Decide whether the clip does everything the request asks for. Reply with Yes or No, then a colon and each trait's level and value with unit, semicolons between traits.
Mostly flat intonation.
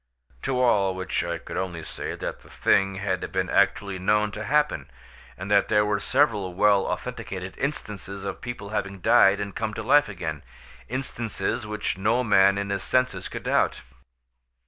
Yes: narrow, 2.1 semitones